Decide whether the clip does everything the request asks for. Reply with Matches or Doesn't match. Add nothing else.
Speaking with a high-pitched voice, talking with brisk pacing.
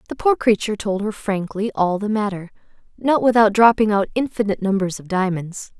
Doesn't match